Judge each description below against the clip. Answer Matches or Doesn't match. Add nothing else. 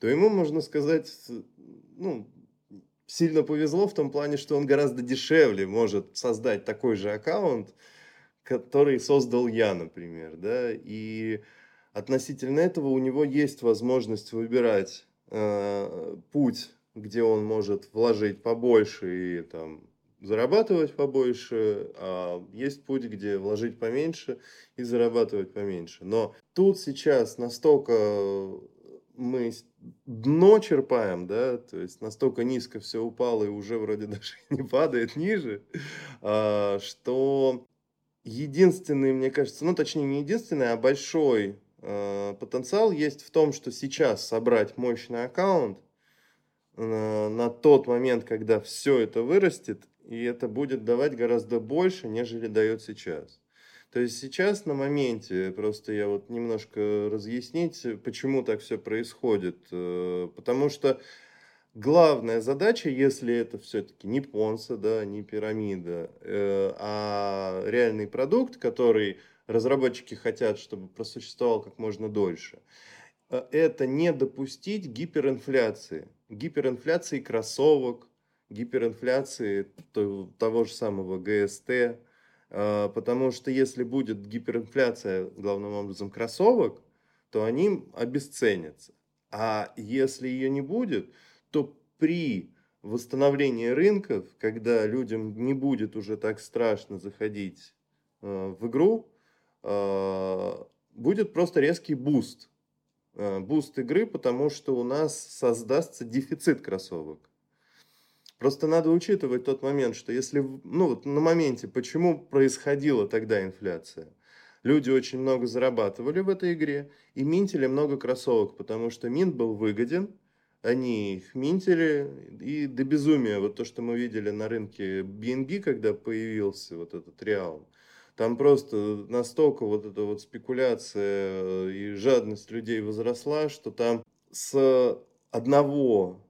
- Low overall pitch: Matches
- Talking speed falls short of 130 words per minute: Matches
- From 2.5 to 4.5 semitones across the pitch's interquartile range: Doesn't match